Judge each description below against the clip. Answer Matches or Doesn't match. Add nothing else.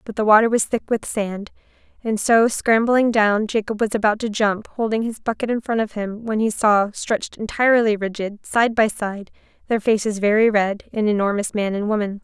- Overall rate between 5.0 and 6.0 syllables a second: Matches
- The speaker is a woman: Matches